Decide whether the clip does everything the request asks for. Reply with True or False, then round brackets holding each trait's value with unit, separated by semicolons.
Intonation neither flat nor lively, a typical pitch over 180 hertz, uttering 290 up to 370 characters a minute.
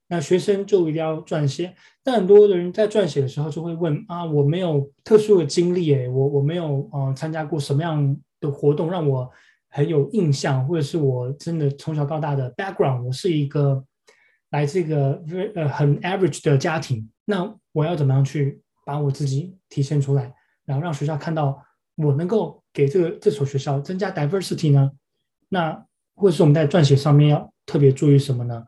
False (4.0 semitones; 150 Hz; 325 characters per minute)